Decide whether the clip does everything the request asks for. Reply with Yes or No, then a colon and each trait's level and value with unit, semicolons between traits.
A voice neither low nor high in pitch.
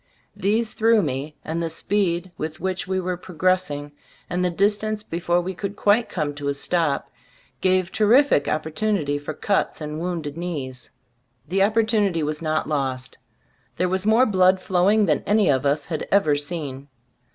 Yes: medium, 175 Hz